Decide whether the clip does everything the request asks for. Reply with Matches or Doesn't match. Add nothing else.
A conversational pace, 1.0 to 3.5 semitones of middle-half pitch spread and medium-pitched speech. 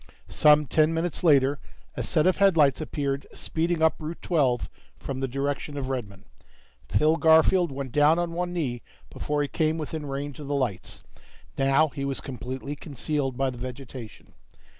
Matches